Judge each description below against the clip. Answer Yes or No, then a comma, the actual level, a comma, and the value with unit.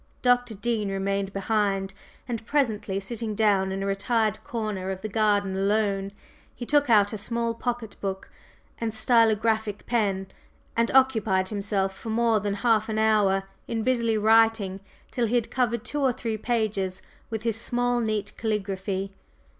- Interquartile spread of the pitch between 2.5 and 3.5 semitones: Yes, average, 2.8 semitones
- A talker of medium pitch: No, high, 215 Hz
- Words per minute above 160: No, average, 155 wpm